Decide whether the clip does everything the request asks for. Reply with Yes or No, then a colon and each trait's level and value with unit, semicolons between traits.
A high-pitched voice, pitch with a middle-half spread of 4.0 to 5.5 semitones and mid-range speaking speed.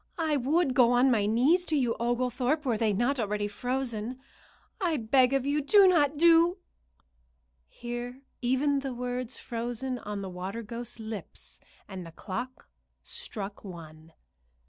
Yes: high, 245 Hz; average, 4.5 semitones; average, 150 wpm